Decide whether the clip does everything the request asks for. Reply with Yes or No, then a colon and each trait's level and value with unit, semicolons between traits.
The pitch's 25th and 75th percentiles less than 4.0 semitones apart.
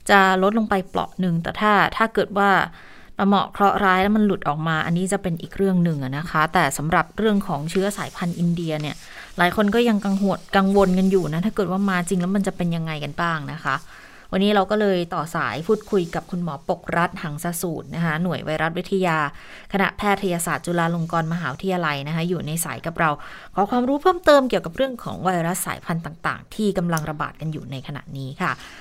Yes: average, 3.3 semitones